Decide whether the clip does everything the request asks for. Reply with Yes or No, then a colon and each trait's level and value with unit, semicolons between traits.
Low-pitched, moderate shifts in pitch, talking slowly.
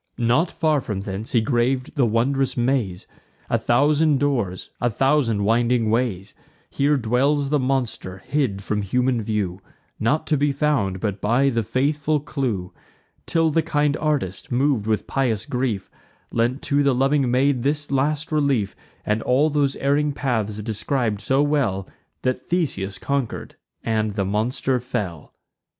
No: low, 125 Hz; average, 4.8 semitones; average, 150 wpm